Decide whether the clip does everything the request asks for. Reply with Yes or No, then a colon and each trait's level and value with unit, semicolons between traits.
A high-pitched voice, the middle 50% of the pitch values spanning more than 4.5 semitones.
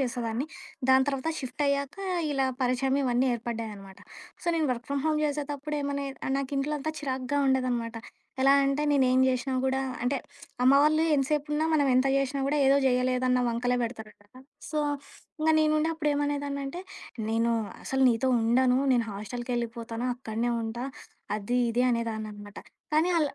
No: very high, 260 Hz; average, 3.0 semitones